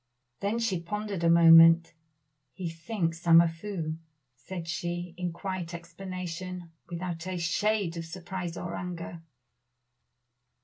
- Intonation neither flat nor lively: No, narrow, 2.0 semitones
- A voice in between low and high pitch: Yes, medium, 175 Hz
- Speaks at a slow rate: Yes, slow, 130 wpm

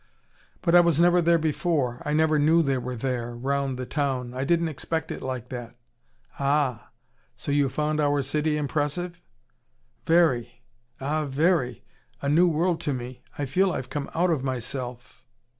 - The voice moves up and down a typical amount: Yes, average, 4.0 semitones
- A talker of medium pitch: Yes, medium, 145 Hz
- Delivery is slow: No, average, 165 wpm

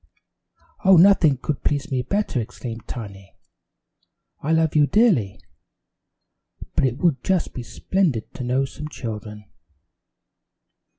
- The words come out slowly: Yes, slow, 120 wpm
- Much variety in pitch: Yes, wide, 5.7 semitones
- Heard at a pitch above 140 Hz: No, low, 135 Hz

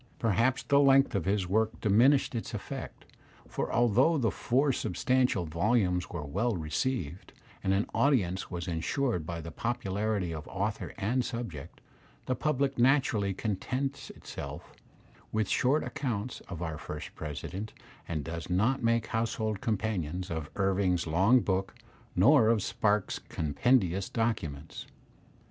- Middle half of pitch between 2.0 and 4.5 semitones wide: No, wide, 5.4 semitones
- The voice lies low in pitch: Yes, low, 105 Hz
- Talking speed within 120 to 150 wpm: Yes, slow, 135 wpm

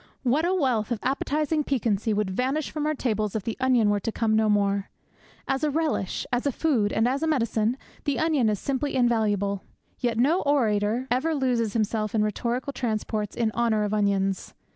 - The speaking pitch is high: Yes, high, 235 Hz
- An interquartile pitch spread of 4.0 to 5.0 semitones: Yes, average, 4.5 semitones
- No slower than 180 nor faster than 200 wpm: Yes, average, 190 wpm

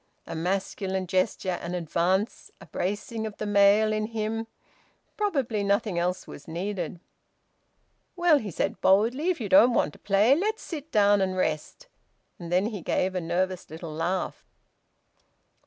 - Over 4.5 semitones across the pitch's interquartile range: No, average, 3.6 semitones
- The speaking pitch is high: Yes, high, 200 Hz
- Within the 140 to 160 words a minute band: Yes, average, 155 wpm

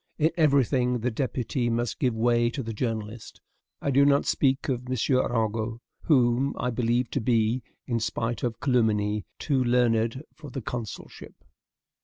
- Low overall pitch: Yes, low, 120 Hz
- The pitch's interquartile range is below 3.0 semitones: Yes, narrow, 2.5 semitones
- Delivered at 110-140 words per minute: No, average, 160 wpm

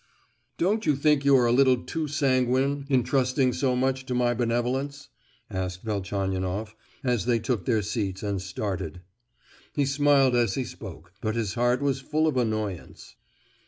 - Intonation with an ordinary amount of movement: Yes, average, 4.4 semitones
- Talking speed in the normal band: Yes, average, 160 wpm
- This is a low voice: Yes, low, 125 Hz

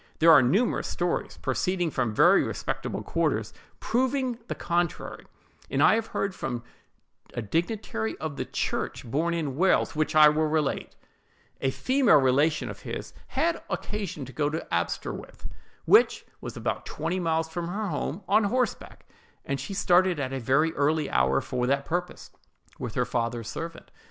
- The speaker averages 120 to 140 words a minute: No, average, 165 wpm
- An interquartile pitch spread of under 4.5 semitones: No, wide, 5.4 semitones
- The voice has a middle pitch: Yes, medium, 160 Hz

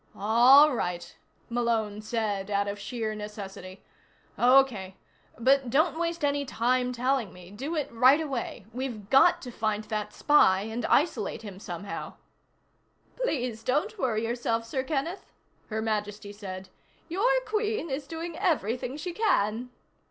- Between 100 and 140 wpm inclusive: Yes, slow, 135 wpm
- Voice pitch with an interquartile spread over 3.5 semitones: Yes, average, 5.2 semitones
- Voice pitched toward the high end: Yes, high, 240 Hz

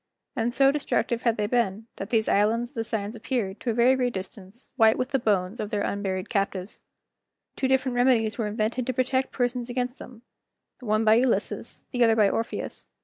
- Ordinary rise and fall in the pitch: Yes, average, 3.0 semitones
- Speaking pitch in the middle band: No, high, 230 Hz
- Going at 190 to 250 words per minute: Yes, fast, 205 wpm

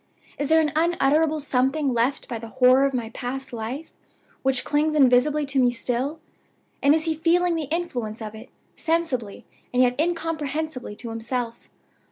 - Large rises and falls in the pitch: No, average, 4.2 semitones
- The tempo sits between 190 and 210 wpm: No, average, 165 wpm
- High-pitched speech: Yes, very high, 270 Hz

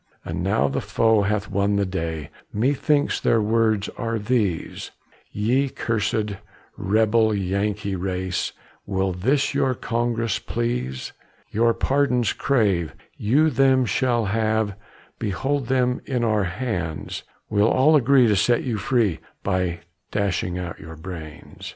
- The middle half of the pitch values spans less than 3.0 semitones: No, average, 4.3 semitones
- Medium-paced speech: No, slow, 130 wpm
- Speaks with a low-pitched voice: Yes, low, 110 Hz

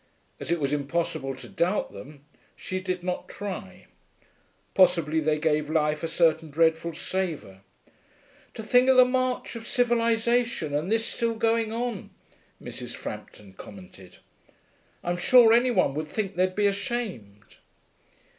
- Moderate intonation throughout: No, wide, 6.9 semitones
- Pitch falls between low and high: Yes, medium, 180 Hz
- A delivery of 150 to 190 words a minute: No, average, 140 wpm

